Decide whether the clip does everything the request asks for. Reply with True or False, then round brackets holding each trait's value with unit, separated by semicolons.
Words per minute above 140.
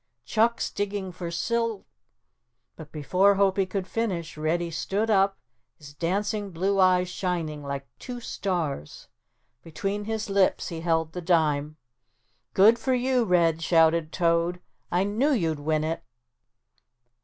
False (135 wpm)